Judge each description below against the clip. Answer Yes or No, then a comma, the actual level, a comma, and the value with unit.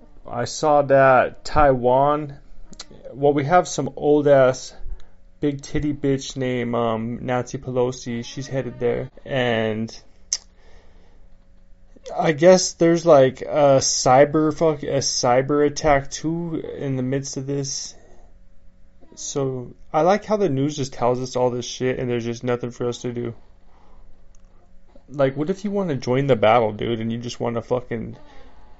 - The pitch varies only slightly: No, average, 4.1 semitones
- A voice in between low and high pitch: No, low, 125 Hz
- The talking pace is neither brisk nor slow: Yes, average, 150 wpm